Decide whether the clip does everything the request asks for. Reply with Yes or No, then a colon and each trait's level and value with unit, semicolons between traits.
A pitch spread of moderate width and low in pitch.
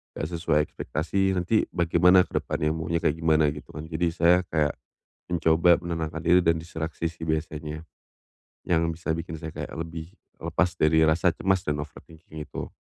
No: narrow, 1.7 semitones; very low, 80 Hz